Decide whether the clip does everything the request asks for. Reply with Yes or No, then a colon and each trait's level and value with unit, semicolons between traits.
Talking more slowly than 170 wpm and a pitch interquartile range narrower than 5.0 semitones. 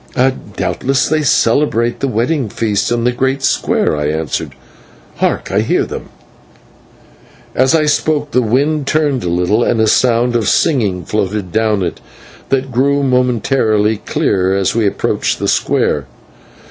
Yes: average, 145 wpm; average, 4.5 semitones